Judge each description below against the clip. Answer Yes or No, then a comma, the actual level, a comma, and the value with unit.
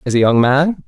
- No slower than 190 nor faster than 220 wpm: No, fast, 275 wpm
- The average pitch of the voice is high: No, medium, 140 Hz